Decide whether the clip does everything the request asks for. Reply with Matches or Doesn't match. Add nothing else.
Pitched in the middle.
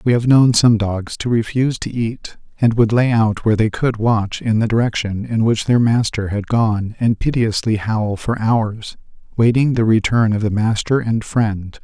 Doesn't match